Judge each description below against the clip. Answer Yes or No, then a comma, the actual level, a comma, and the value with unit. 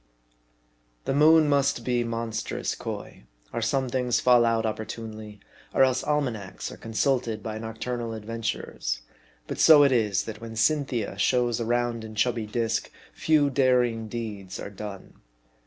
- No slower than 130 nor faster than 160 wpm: Yes, average, 150 wpm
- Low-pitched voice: Yes, low, 115 Hz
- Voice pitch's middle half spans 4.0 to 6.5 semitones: No, narrow, 2.5 semitones